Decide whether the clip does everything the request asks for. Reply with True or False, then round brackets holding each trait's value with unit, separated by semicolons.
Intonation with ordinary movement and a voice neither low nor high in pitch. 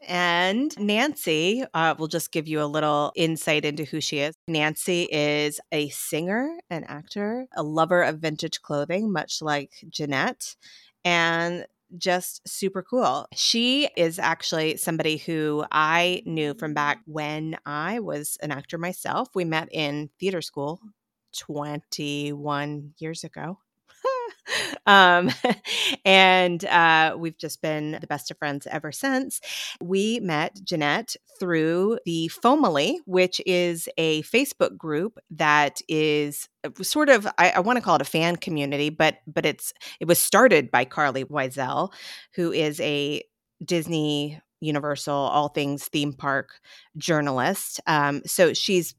True (3.5 semitones; 160 Hz)